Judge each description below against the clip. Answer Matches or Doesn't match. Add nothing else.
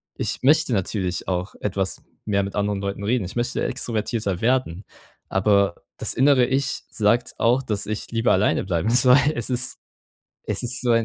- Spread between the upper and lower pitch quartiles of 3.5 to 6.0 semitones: Matches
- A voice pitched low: Matches